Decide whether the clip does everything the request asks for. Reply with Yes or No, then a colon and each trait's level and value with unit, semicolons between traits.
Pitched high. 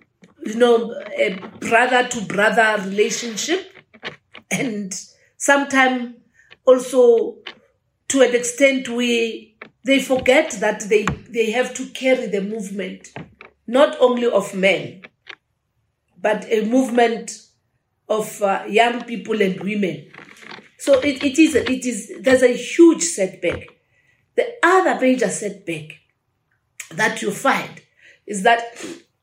Yes: high, 230 Hz